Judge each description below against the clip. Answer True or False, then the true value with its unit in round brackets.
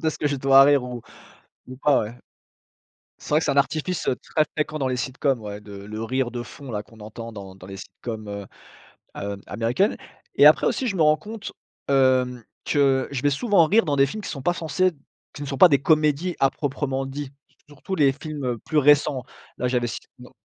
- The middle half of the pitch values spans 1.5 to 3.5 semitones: False (3.9 semitones)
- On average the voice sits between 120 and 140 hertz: True (135 Hz)